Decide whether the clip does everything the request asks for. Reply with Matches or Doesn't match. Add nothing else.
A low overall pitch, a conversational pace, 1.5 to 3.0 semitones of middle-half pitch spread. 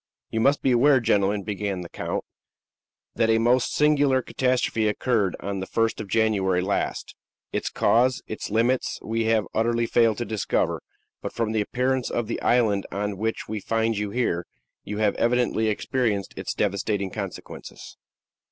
Matches